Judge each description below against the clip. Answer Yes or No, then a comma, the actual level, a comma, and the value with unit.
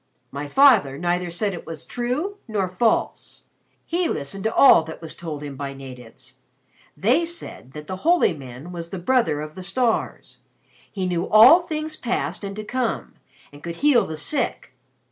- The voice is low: No, medium, 185 Hz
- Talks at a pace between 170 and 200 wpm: Yes, average, 175 wpm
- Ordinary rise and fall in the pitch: No, wide, 8.4 semitones